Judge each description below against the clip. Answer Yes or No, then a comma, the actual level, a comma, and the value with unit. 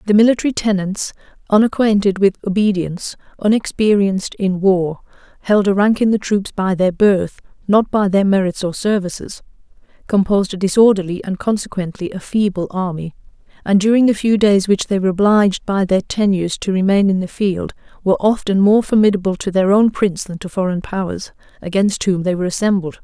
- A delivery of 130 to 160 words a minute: No, average, 170 wpm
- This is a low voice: No, high, 195 Hz